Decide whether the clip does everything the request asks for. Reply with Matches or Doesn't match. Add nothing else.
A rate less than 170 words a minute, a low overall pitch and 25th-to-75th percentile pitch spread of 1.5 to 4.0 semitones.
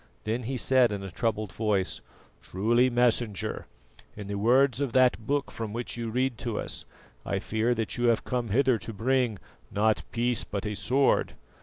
Doesn't match